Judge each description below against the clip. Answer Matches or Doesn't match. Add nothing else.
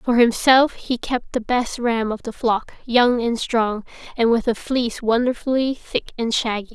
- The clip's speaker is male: Doesn't match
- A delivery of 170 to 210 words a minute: Matches